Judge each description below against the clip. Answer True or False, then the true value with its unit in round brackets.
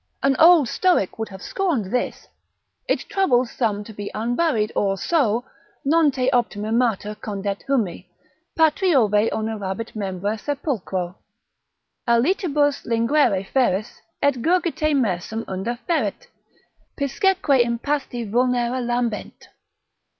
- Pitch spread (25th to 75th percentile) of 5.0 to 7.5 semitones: True (5.3 semitones)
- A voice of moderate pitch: False (240 Hz)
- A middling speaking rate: False (110 wpm)